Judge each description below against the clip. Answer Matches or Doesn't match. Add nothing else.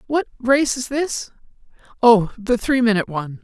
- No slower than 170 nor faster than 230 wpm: Doesn't match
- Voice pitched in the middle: Doesn't match